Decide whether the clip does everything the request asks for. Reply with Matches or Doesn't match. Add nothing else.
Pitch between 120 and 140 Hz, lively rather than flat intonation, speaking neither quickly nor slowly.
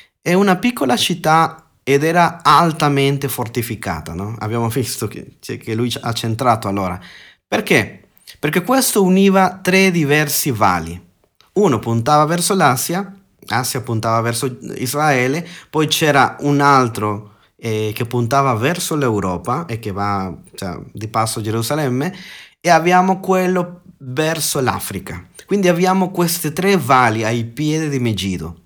Matches